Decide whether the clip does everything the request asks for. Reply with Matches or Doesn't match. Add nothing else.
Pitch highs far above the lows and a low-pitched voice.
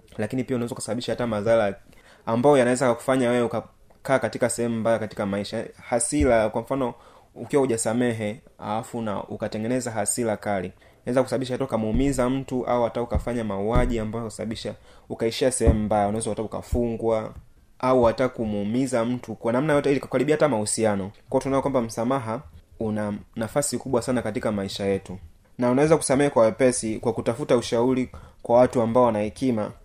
Doesn't match